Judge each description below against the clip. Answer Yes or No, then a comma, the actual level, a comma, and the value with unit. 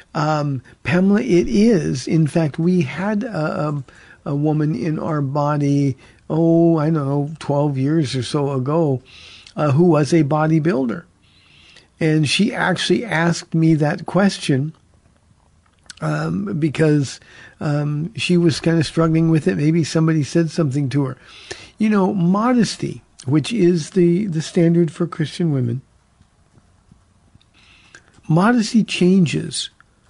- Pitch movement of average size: Yes, average, 3.4 semitones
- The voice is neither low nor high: Yes, medium, 160 Hz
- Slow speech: Yes, slow, 130 wpm